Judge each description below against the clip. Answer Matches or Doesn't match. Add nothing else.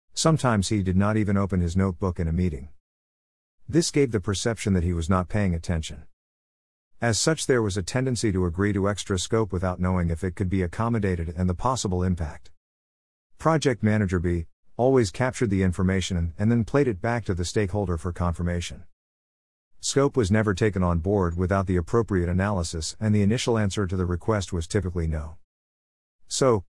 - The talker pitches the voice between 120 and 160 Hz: Doesn't match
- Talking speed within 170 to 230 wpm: Matches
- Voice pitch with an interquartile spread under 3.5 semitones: Doesn't match